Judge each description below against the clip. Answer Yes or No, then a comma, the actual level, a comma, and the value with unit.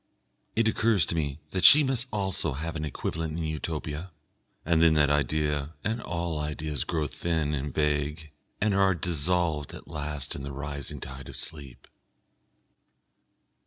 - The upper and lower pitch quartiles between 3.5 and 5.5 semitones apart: No, average, 2.7 semitones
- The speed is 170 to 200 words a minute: No, average, 155 wpm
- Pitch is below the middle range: Yes, very low, 75 Hz